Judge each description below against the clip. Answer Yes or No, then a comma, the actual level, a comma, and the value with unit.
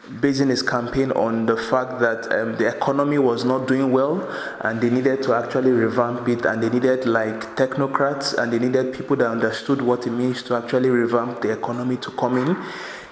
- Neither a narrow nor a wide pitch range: No, narrow, 1.9 semitones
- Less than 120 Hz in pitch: No, low, 125 Hz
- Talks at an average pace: Yes, average, 195 wpm